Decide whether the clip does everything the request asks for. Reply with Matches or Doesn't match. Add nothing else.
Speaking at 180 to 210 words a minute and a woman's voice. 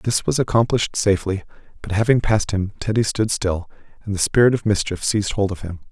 Doesn't match